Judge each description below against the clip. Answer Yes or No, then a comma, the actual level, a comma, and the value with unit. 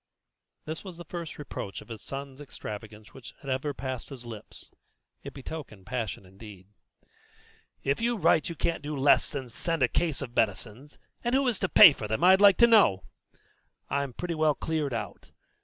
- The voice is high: No, medium, 140 Hz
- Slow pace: No, average, 185 wpm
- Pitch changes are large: Yes, wide, 6.4 semitones